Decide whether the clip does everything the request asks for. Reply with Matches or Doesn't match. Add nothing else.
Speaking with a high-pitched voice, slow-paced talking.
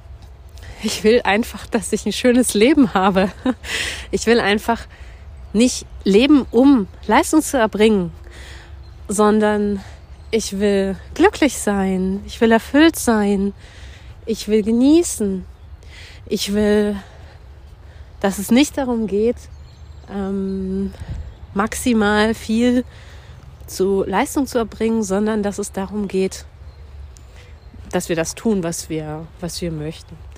Matches